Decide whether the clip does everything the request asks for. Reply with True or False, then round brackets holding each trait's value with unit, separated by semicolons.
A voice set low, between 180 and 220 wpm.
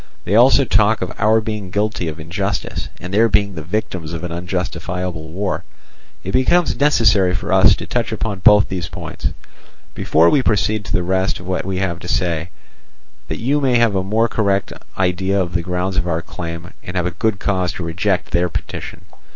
True (95 Hz; 195 wpm)